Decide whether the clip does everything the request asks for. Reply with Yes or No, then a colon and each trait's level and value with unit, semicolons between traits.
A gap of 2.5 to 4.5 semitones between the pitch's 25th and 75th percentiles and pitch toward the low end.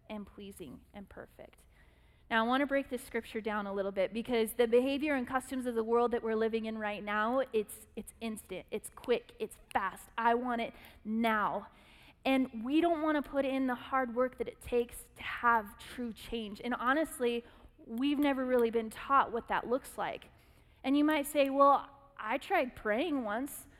No: average, 3.4 semitones; high, 240 Hz